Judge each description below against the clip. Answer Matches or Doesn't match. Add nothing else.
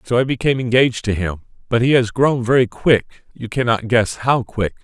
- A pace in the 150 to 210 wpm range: Matches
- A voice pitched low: Matches